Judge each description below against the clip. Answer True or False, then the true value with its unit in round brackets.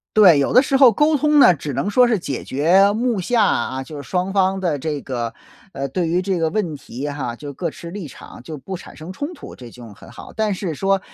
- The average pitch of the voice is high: False (180 Hz)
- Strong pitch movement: True (6.3 semitones)